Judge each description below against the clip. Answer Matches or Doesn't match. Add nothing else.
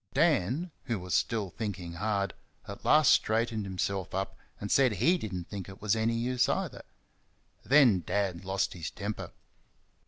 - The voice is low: Matches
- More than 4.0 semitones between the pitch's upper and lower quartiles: Doesn't match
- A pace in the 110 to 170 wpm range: Matches